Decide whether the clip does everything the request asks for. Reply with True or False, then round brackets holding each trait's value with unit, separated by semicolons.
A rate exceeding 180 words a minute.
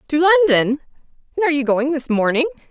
False (155 wpm)